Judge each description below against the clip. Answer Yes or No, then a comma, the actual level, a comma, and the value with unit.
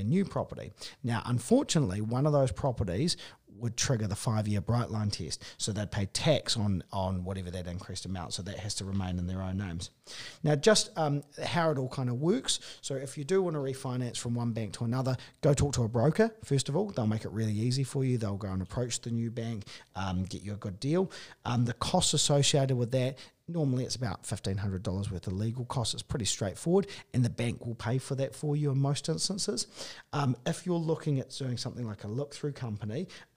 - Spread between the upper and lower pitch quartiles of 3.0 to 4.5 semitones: No, wide, 5.4 semitones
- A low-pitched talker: Yes, low, 120 Hz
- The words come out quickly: Yes, fast, 225 wpm